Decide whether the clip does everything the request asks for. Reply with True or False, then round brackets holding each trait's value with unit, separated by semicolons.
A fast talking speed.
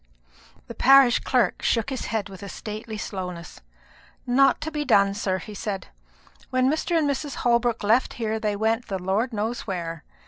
False (175 wpm)